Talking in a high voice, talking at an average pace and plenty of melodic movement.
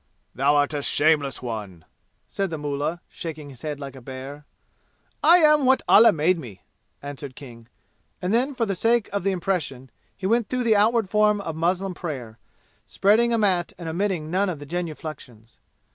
No: medium, 165 Hz; average, 180 wpm; wide, 6.3 semitones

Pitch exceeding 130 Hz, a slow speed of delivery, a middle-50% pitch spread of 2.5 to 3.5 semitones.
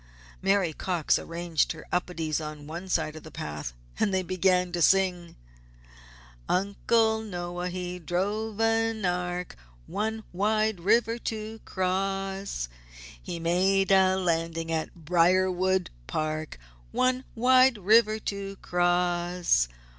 Yes: medium, 185 Hz; slow, 115 wpm; average, 2.8 semitones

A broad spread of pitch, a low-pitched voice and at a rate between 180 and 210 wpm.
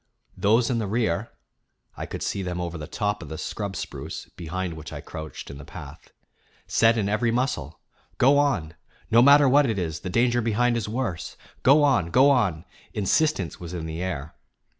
Yes: wide, 6.2 semitones; low, 105 Hz; average, 190 wpm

